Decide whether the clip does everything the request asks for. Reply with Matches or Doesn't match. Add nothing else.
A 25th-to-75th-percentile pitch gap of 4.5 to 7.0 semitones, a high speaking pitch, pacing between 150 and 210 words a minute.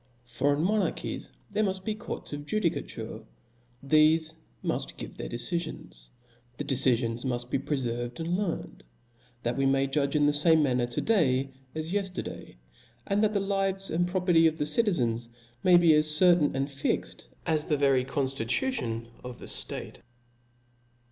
Doesn't match